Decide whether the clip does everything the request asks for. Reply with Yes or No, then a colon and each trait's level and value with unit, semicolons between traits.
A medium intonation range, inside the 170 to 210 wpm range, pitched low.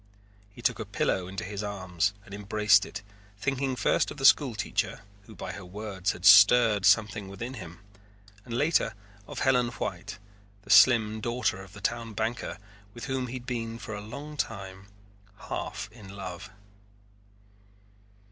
No: average, 3.5 semitones; average, 160 wpm; low, 105 Hz